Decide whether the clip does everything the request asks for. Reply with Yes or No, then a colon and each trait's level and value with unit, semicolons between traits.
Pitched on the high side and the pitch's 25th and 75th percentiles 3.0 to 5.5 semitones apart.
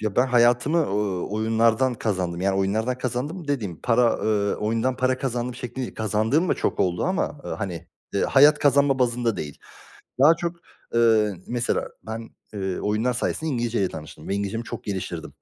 No: low, 115 Hz; average, 4.0 semitones